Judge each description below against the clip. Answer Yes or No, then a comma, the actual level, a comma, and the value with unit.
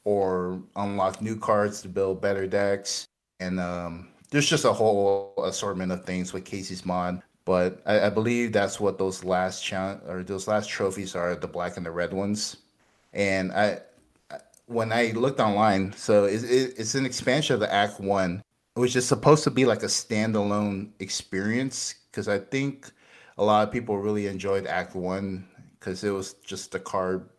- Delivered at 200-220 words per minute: No, average, 175 wpm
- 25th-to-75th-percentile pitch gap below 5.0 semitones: Yes, narrow, 2.6 semitones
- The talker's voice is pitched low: Yes, low, 100 Hz